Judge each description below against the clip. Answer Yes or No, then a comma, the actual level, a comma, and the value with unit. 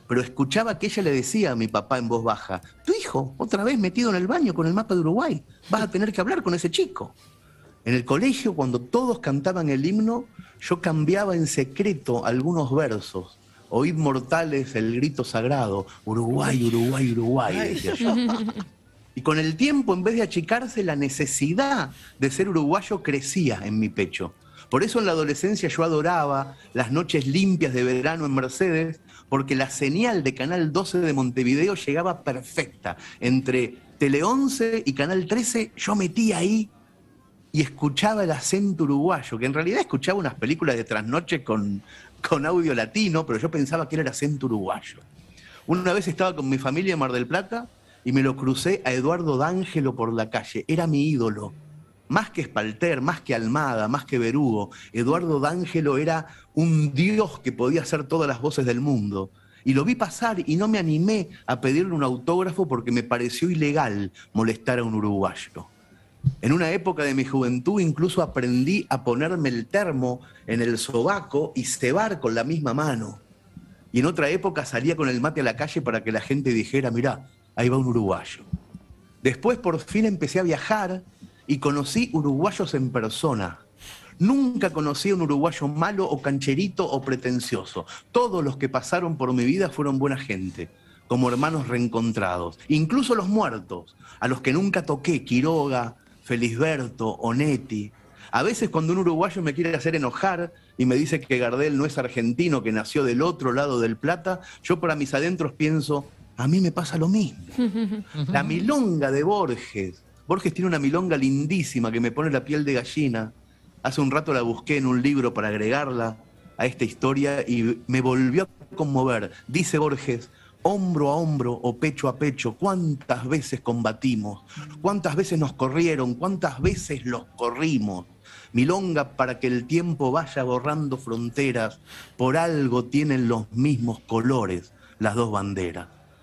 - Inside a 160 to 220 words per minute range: Yes, average, 170 wpm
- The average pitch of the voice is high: No, medium, 140 Hz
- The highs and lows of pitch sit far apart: Yes, wide, 5.8 semitones